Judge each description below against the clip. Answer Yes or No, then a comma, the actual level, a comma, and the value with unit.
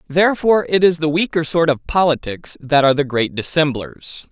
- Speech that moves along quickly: No, average, 180 wpm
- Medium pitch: Yes, medium, 155 Hz